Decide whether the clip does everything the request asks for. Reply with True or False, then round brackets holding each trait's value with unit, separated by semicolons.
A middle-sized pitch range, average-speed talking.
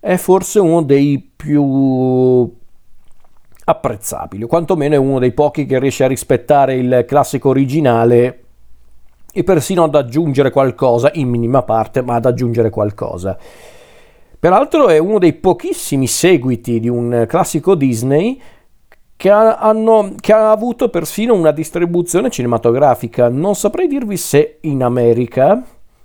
False (6.3 semitones; 130 wpm)